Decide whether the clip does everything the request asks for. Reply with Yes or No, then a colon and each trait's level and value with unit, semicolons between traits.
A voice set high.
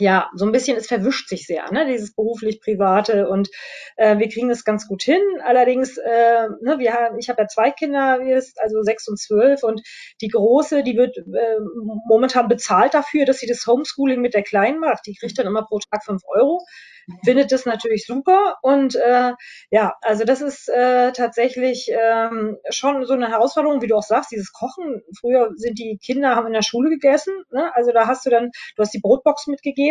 Yes: high, 240 Hz